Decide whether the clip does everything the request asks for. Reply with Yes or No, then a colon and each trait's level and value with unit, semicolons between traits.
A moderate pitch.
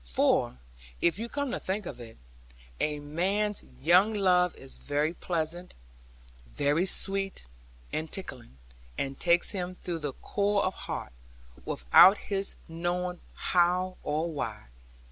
Yes: medium, 175 Hz